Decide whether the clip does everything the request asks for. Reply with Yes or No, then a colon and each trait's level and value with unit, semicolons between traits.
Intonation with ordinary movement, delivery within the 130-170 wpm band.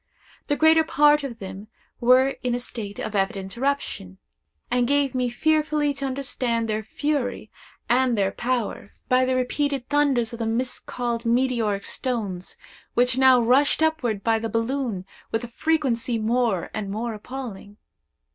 Yes: average, 3.4 semitones; average, 150 wpm